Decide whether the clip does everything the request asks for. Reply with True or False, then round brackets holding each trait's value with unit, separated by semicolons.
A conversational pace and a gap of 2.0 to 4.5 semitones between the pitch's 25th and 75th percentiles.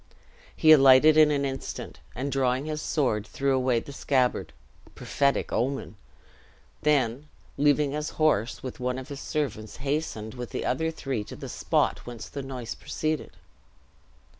True (150 wpm; 3.0 semitones)